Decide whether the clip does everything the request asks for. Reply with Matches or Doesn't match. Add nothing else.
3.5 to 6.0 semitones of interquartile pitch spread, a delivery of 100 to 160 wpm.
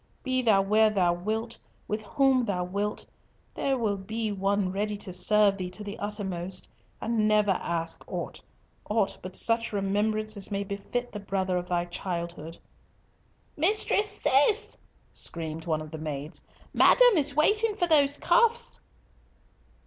Matches